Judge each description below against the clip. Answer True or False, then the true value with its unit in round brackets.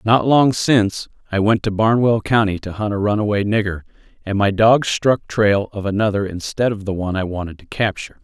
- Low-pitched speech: True (105 Hz)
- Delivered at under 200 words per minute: False (205 wpm)